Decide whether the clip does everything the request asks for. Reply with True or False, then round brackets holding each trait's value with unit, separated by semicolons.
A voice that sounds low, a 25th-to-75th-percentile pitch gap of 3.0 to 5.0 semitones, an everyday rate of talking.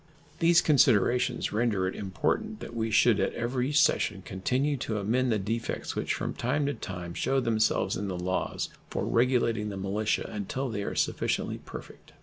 True (115 Hz; 4.1 semitones; 170 wpm)